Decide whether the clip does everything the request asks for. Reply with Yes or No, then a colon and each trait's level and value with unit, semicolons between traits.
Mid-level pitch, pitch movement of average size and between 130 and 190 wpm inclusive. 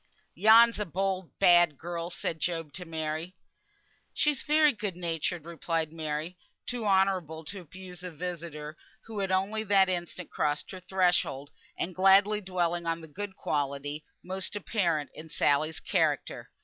Yes: medium, 175 Hz; average, 3.2 semitones; average, 150 wpm